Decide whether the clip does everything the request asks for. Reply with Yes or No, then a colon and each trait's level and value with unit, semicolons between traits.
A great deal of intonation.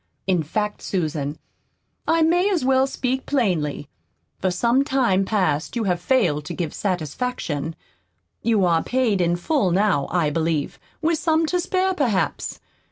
Yes: wide, 7.9 semitones